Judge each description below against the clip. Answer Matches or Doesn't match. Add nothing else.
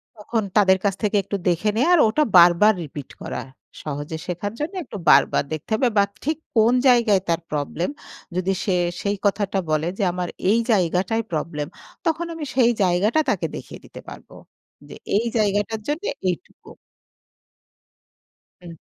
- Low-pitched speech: Doesn't match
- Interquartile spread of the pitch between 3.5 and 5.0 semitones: Matches